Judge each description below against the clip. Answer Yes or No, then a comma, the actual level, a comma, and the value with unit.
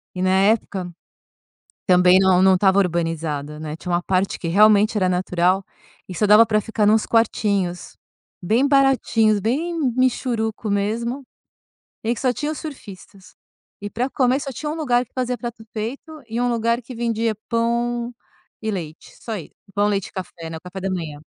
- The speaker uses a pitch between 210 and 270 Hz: Yes, high, 215 Hz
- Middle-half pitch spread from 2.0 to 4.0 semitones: No, average, 4.4 semitones